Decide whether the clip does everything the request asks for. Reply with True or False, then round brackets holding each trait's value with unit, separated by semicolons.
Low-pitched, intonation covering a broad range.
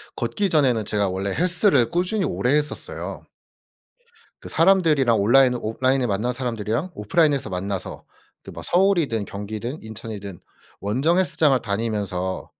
True (120 Hz; 7.0 semitones)